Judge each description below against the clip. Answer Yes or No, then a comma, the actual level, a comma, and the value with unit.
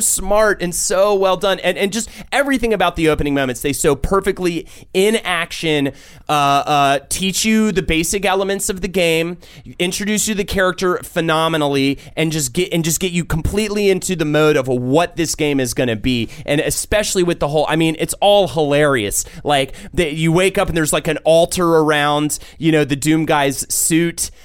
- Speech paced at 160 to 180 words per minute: No, average, 190 wpm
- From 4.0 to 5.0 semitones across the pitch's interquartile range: Yes, average, 4.4 semitones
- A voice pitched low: No, medium, 165 Hz